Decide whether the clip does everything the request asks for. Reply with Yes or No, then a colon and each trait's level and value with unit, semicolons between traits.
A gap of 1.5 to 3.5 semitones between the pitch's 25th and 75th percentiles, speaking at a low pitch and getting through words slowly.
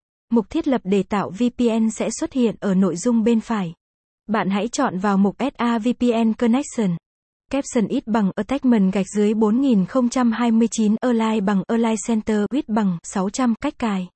No: average, 2.8 semitones; high, 225 Hz; slow, 160 wpm